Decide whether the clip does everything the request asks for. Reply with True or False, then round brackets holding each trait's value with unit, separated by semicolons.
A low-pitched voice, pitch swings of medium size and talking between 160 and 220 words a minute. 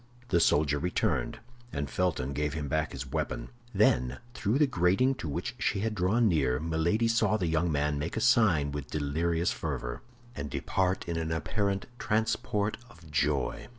False (80 Hz; 5.8 semitones; 170 wpm)